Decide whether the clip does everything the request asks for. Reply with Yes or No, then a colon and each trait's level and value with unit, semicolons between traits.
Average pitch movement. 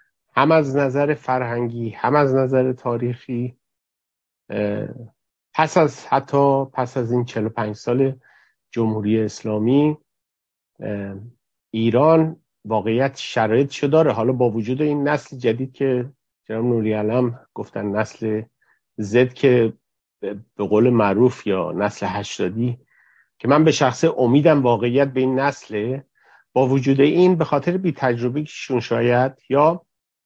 Yes: average, 3.6 semitones